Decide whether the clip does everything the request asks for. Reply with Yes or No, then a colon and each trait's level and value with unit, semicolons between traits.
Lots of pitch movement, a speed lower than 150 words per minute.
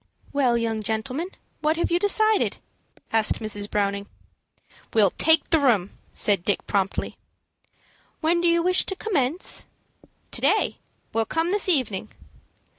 Yes: wide, 8.1 semitones; slow, 135 wpm